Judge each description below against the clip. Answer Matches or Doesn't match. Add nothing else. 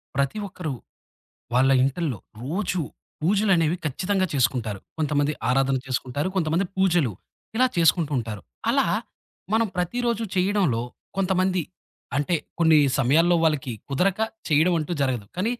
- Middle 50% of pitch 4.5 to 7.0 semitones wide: Matches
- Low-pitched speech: Doesn't match